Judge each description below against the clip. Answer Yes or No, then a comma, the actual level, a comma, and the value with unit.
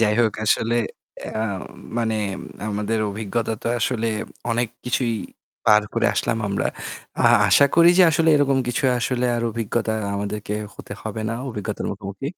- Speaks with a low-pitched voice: Yes, low, 115 Hz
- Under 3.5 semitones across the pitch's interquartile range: Yes, narrow, 2.5 semitones